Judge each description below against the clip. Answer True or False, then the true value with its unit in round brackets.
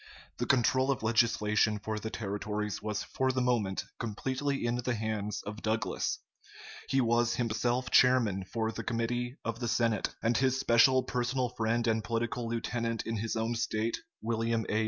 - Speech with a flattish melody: True (2.0 semitones)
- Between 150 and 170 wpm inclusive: True (165 wpm)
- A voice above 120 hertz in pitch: False (115 Hz)